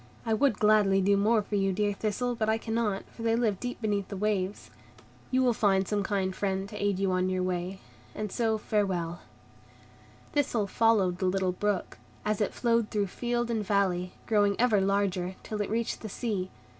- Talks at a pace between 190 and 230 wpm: Yes, average, 195 wpm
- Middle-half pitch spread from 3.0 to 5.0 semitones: No, narrow, 2.5 semitones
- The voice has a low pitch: No, high, 205 Hz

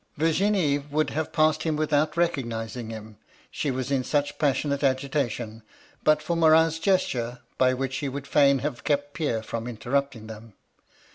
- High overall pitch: No, medium, 140 Hz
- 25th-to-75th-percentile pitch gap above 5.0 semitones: No, average, 4.0 semitones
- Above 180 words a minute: No, average, 155 wpm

